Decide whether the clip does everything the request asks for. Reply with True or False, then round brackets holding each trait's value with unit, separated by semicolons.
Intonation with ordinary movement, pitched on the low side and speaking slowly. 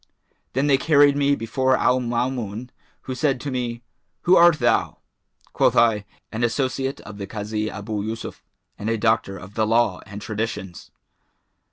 False (3.8 semitones; 115 Hz; 160 wpm)